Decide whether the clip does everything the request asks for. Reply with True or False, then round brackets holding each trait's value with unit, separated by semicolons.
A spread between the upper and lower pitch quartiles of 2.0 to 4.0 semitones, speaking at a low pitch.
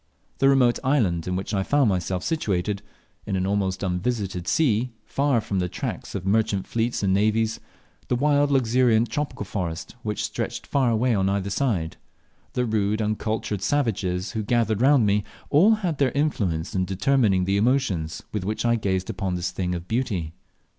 False (4.8 semitones; 105 Hz)